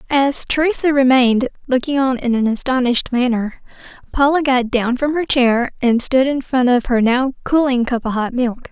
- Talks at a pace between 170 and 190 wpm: Yes, average, 185 wpm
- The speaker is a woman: Yes, female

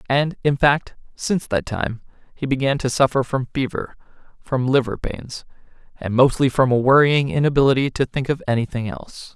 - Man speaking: Yes, male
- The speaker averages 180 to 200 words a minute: No, average, 165 wpm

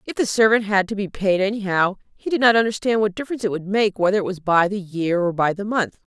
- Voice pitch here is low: No, high, 200 Hz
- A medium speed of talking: No, fast, 265 wpm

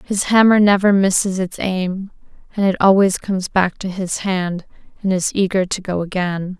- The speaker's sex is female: Yes, female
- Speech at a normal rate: Yes, average, 180 wpm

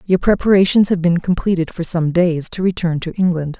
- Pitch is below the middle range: No, medium, 175 Hz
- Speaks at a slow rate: No, average, 200 wpm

